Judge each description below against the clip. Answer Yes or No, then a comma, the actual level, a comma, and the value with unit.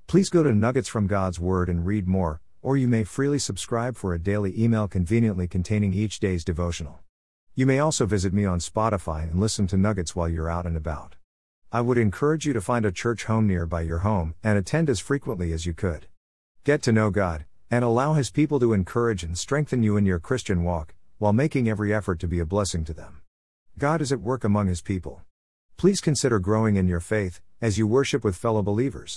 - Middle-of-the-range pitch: No, low, 100 Hz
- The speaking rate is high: Yes, fast, 220 wpm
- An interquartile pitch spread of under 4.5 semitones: No, average, 5.1 semitones